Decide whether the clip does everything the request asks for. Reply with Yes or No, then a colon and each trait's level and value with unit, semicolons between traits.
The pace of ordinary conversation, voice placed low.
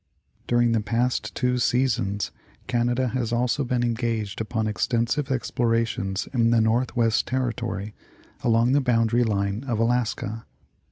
No: slow, 125 wpm; low, 115 Hz